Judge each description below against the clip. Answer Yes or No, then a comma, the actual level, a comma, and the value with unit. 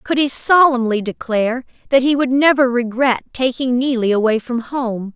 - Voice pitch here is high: Yes, very high, 250 Hz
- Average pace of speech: Yes, average, 165 wpm